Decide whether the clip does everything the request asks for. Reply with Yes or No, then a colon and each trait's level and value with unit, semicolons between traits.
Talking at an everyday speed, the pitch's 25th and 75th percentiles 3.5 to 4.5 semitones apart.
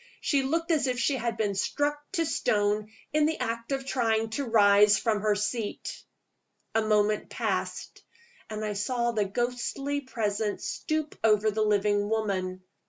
Yes: average, 160 wpm; average, 4.2 semitones